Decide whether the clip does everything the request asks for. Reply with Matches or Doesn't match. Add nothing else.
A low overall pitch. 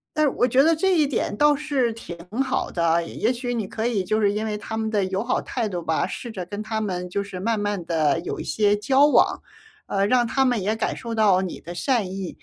Doesn't match